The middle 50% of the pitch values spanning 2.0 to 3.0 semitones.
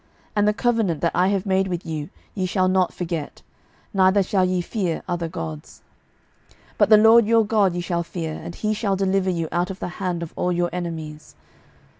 Yes: narrow, 2.5 semitones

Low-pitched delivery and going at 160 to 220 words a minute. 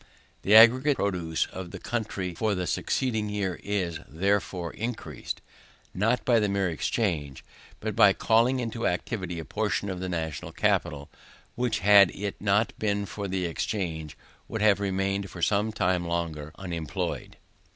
No: low, 100 Hz; average, 150 wpm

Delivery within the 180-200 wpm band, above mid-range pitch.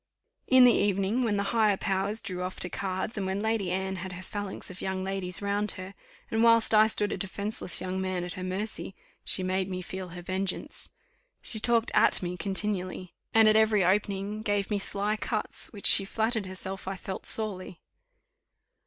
Yes: average, 190 wpm; high, 195 Hz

